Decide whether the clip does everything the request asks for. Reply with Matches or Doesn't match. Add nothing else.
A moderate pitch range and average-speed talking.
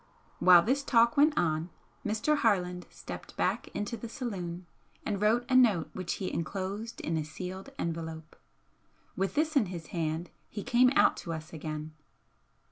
Doesn't match